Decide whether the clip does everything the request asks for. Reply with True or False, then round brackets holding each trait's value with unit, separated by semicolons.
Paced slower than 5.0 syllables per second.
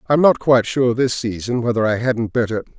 False (5.4 syllables/s)